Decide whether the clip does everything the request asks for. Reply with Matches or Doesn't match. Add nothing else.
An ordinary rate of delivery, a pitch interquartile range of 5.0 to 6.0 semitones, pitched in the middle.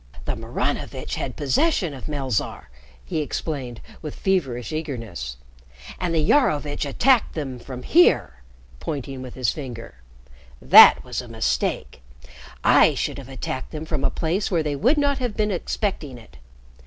Matches